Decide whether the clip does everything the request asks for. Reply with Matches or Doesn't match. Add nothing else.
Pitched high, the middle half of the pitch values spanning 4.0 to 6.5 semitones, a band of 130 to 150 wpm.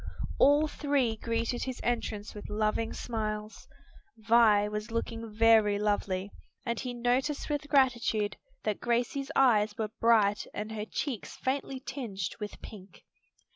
Doesn't match